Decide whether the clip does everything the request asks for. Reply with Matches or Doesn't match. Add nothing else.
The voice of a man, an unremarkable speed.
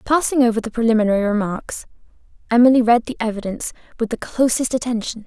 Doesn't match